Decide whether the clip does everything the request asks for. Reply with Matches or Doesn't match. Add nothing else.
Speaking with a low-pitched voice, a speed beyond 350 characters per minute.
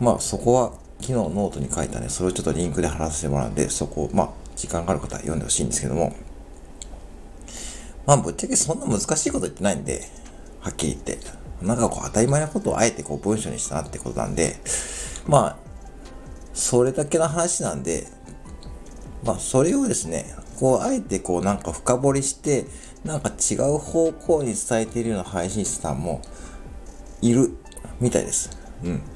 Matches